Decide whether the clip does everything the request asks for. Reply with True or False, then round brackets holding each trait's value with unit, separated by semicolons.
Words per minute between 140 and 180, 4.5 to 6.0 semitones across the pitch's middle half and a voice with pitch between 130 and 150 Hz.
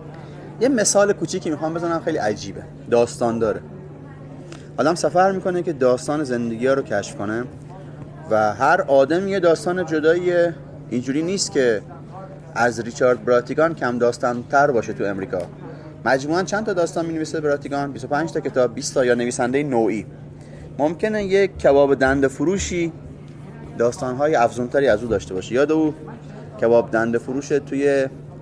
True (145 wpm; 5.1 semitones; 140 Hz)